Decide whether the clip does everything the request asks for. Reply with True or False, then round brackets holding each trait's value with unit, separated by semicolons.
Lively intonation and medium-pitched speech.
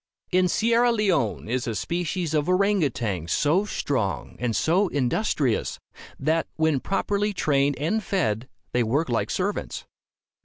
True (7.6 semitones; 160 Hz)